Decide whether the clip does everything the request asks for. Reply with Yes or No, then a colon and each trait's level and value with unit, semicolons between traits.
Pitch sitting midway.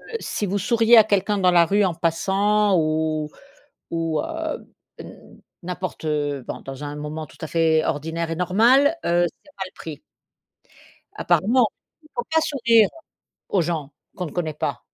Yes: medium, 175 Hz